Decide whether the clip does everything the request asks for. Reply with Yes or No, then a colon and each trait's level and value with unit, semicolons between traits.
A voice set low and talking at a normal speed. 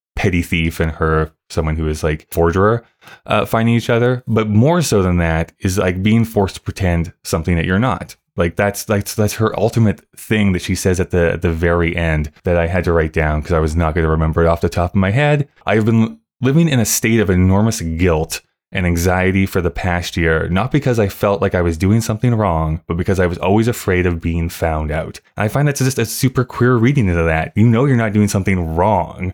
No: very low, 95 Hz; fast, 240 wpm